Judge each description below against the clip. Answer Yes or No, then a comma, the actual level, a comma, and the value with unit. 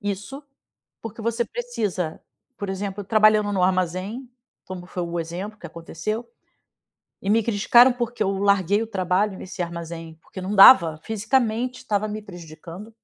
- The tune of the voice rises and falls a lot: No, average, 3.6 semitones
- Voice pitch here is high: Yes, high, 200 Hz